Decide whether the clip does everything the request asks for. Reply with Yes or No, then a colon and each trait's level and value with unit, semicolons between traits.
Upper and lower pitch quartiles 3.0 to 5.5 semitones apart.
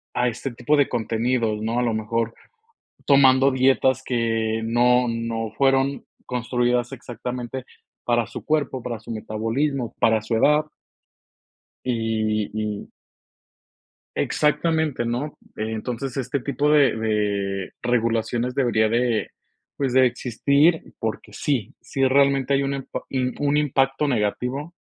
Yes: average, 3.3 semitones